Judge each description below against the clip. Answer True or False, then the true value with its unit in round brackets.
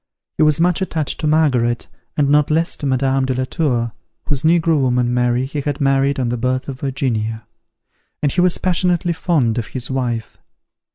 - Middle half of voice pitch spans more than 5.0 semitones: False (3.9 semitones)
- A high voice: False (135 Hz)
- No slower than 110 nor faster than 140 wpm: False (185 wpm)